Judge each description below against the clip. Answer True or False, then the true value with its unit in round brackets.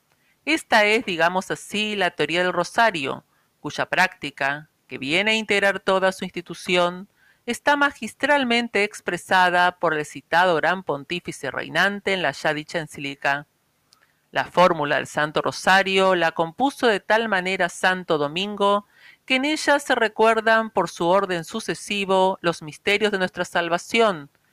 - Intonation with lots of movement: False (3.8 semitones)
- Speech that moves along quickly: False (140 wpm)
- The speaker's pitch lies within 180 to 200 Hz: True (185 Hz)